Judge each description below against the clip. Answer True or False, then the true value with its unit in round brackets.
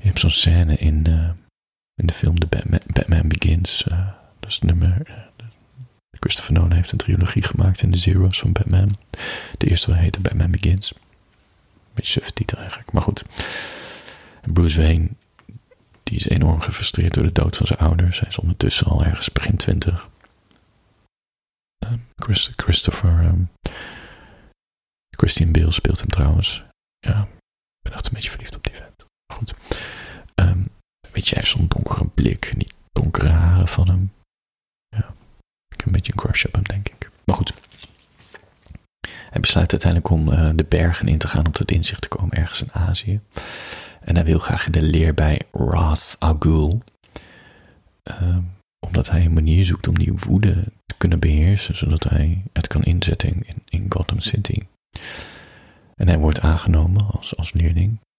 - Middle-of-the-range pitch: False (90 Hz)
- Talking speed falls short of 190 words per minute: True (170 wpm)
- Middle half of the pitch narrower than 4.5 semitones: True (3.4 semitones)